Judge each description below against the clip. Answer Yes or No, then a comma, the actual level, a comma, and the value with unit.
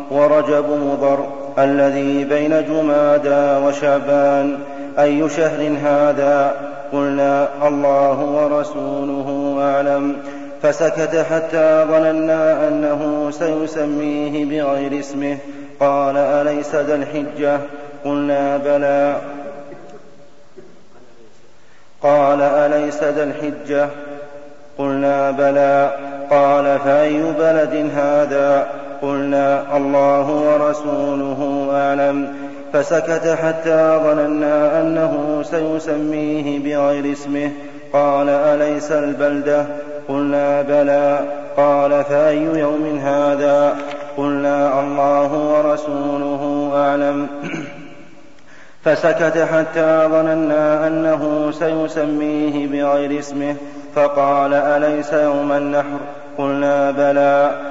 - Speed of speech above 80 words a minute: No, average, 75 wpm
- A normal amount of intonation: No, narrow, 1.0 semitones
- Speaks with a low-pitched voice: No, medium, 145 Hz